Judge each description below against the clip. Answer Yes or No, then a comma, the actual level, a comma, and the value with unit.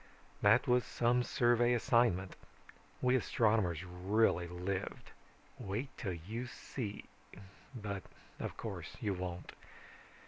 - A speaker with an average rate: No, slow, 105 wpm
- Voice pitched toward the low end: Yes, low, 105 Hz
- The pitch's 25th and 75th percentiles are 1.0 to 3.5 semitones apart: No, average, 4.8 semitones